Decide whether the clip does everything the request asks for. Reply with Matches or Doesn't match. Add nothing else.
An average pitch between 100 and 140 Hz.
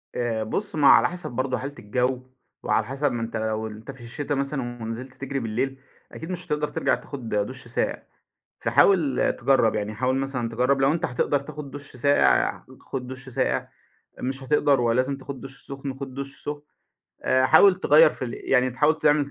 Matches